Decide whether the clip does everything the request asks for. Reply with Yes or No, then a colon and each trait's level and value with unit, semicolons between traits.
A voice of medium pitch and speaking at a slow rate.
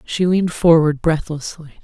Yes: medium, 160 Hz; slow, 130 wpm